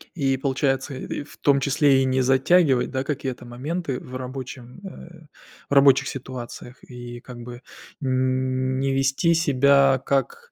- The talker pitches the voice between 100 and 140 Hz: Yes, low, 135 Hz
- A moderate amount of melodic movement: No, narrow, 1.5 semitones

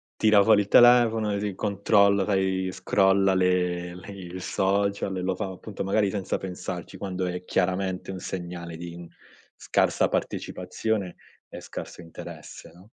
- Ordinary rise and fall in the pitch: No, narrow, 1.7 semitones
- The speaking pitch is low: Yes, very low, 95 Hz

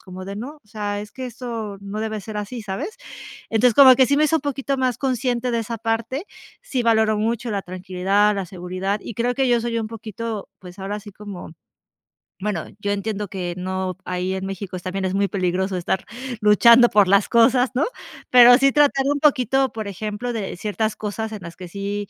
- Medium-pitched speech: No, high, 215 Hz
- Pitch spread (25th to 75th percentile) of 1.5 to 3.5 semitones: No, average, 3.9 semitones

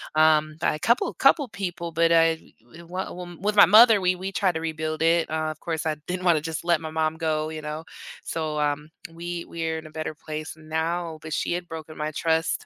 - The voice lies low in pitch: No, medium, 160 Hz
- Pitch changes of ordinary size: No, narrow, 1.8 semitones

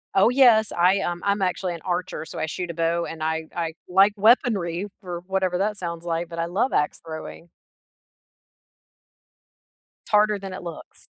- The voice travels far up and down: No, average, 2.9 semitones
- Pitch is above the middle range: No, medium, 180 Hz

